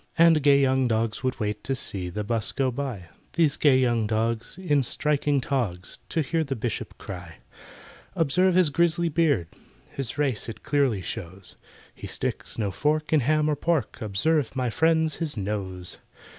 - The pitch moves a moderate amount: No, wide, 6.0 semitones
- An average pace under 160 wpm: No, average, 170 wpm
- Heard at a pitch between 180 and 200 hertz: No, low, 130 Hz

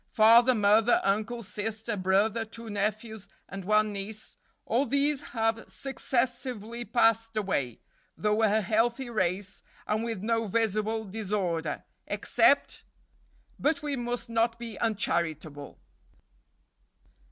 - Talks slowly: Yes, slow, 110 wpm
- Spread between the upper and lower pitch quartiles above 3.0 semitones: No, narrow, 2.4 semitones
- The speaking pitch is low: No, high, 220 Hz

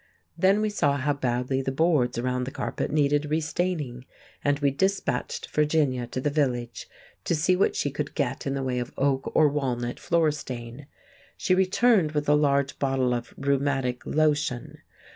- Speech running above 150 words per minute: Yes, average, 175 wpm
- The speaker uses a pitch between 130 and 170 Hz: Yes, medium, 140 Hz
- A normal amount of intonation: Yes, average, 3.1 semitones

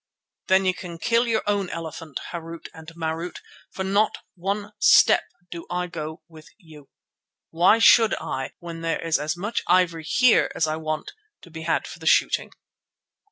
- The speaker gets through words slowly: No, average, 170 wpm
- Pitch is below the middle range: No, medium, 170 Hz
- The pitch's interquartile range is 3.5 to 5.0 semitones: No, average, 3.1 semitones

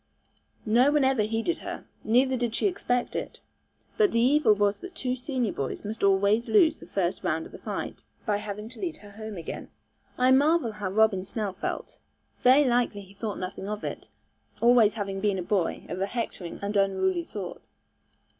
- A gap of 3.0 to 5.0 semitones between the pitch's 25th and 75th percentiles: Yes, average, 4.0 semitones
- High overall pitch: Yes, high, 215 Hz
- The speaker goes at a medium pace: Yes, average, 190 wpm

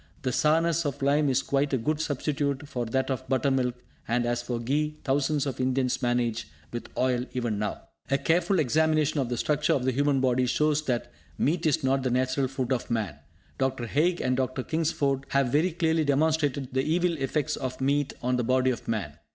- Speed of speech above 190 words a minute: Yes, average, 200 wpm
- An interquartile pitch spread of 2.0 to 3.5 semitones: Yes, average, 3.1 semitones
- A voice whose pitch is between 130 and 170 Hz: Yes, low, 135 Hz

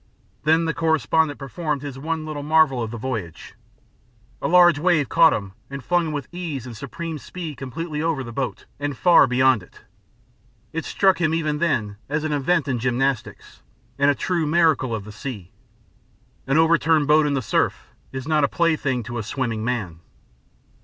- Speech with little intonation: No, average, 4.2 semitones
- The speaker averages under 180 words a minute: No, average, 185 wpm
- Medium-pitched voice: Yes, medium, 145 Hz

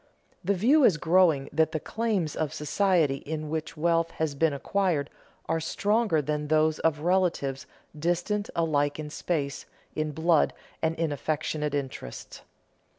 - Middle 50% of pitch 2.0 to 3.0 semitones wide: Yes, average, 2.7 semitones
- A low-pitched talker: No, medium, 160 Hz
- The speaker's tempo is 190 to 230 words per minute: No, average, 150 wpm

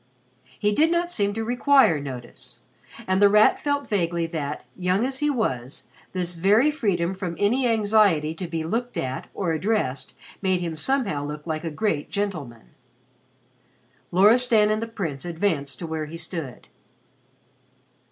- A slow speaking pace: No, average, 150 wpm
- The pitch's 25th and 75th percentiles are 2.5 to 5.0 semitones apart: No, wide, 5.6 semitones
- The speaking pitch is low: No, medium, 185 Hz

